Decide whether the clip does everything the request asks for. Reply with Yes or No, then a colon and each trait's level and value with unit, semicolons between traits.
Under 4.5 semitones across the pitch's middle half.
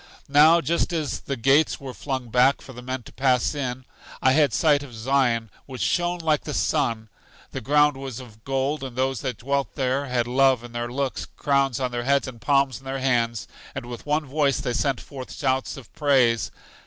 Yes: narrow, 2.4 semitones